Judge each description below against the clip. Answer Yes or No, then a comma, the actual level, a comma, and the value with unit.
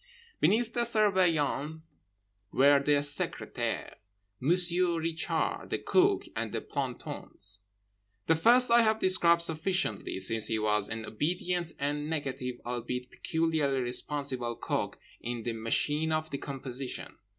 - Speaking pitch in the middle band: Yes, medium, 150 Hz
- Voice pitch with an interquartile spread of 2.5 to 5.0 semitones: No, wide, 5.6 semitones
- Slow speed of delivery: Yes, slow, 115 wpm